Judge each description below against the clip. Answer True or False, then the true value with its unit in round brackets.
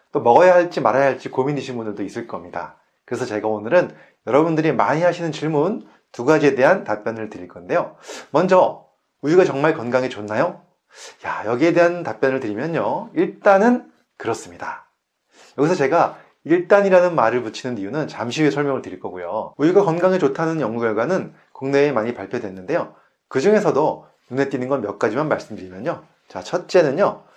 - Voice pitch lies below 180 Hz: True (140 Hz)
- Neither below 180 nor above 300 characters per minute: False (375 characters per minute)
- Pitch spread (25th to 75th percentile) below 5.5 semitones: False (6.2 semitones)